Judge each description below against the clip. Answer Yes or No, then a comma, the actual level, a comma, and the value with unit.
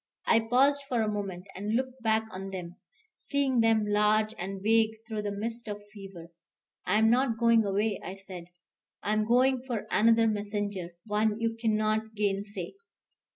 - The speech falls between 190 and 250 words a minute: No, average, 165 wpm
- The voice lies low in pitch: No, high, 215 Hz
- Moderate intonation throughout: No, narrow, 2.1 semitones